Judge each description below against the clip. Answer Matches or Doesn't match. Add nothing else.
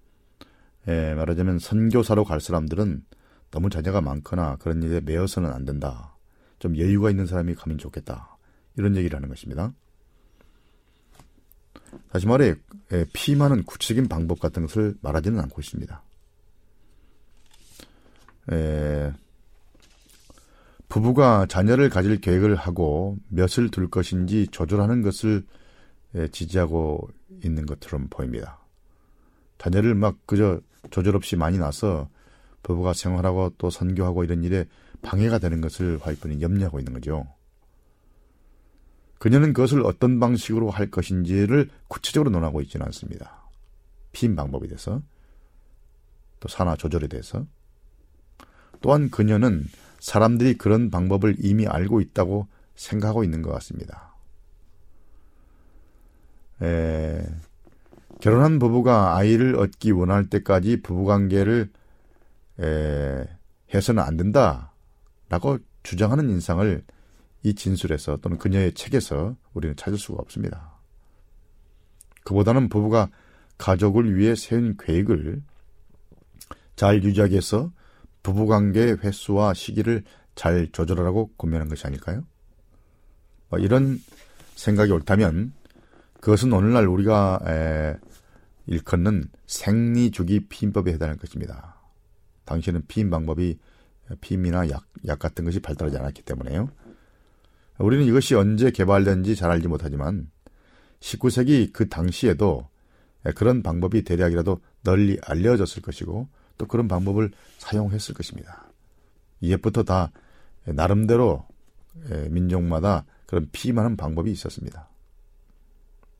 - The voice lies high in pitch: Doesn't match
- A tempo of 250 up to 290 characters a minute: Matches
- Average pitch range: Matches